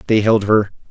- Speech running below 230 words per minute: Yes, average, 200 wpm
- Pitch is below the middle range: Yes, low, 105 Hz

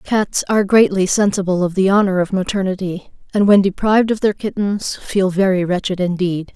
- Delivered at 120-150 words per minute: No, average, 175 wpm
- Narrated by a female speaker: Yes, female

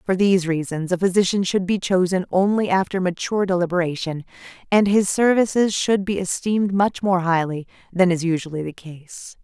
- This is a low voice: No, medium, 185 Hz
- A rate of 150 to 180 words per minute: Yes, average, 165 wpm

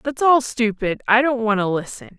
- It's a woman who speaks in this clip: Yes, female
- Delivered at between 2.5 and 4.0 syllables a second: No, 4.9 syllables/s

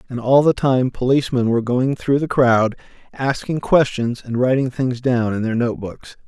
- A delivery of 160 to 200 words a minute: Yes, average, 180 wpm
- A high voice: No, low, 125 Hz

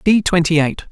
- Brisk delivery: No, average, 195 wpm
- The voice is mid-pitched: Yes, medium, 170 Hz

